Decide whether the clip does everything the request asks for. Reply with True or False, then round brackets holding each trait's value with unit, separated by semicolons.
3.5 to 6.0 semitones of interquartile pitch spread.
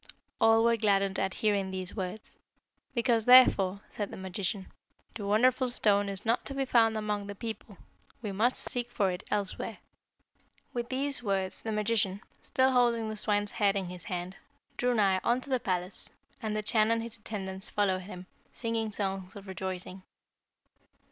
False (3.1 semitones)